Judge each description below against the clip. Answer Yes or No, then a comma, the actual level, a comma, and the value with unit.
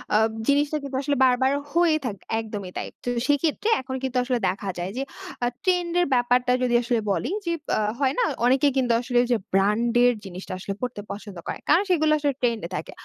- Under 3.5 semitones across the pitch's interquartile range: No, average, 4.4 semitones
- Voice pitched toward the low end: No, very high, 250 Hz